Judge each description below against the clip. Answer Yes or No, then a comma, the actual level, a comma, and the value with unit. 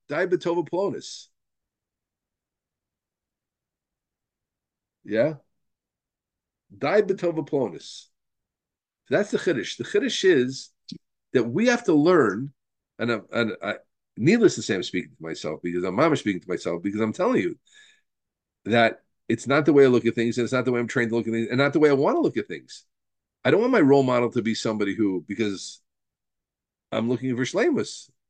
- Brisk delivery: No, average, 175 wpm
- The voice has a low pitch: Yes, low, 125 Hz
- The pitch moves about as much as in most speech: No, wide, 6.4 semitones